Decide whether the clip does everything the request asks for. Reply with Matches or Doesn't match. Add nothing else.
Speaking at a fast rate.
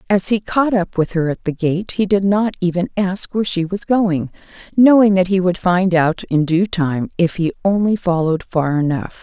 Matches